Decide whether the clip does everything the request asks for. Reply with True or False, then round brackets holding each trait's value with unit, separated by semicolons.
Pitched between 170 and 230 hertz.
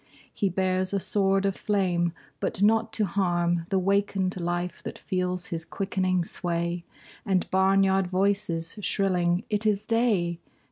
True (185 Hz)